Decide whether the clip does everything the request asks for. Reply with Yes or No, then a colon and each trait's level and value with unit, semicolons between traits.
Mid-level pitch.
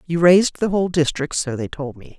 Yes: medium, 160 Hz